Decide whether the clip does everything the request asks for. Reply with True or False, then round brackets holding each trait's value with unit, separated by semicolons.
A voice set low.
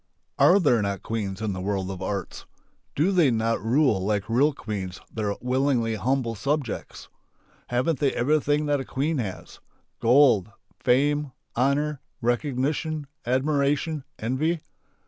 True (130 Hz)